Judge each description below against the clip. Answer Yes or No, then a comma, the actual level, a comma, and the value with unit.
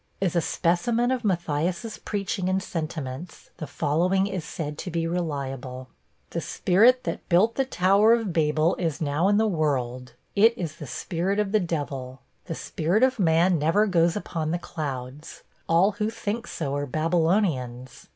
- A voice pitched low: No, medium, 170 Hz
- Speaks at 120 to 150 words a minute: No, average, 165 wpm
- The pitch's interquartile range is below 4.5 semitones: No, average, 4.8 semitones